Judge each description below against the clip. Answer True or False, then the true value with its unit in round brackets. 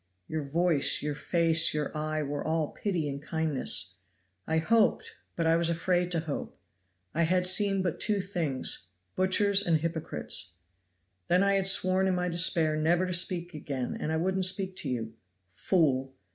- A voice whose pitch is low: False (165 Hz)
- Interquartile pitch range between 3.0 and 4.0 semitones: True (3.3 semitones)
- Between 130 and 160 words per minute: False (170 wpm)